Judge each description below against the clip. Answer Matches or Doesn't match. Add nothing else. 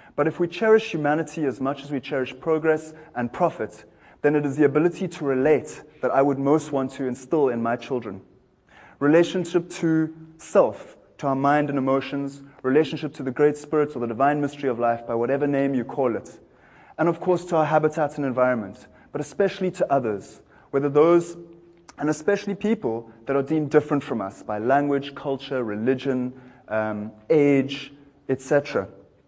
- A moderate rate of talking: Matches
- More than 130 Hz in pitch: Matches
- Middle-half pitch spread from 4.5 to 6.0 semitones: Doesn't match